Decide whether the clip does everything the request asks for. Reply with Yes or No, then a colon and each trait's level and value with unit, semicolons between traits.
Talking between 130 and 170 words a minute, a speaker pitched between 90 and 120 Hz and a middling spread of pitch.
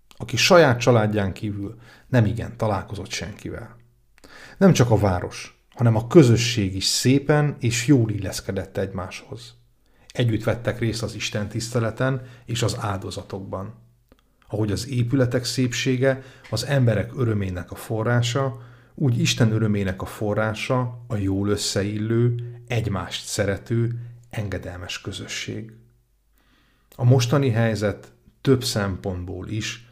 No: average, 115 wpm; low, 115 Hz; average, 3.2 semitones